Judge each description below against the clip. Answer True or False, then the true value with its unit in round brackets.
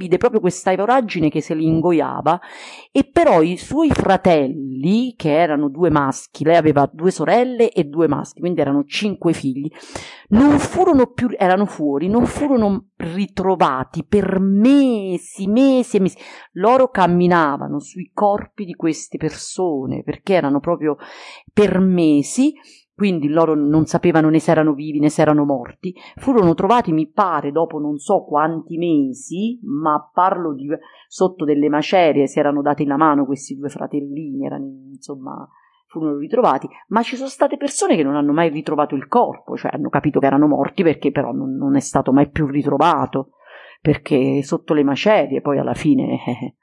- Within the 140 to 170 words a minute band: True (160 wpm)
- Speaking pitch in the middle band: True (170 Hz)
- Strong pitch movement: True (5.8 semitones)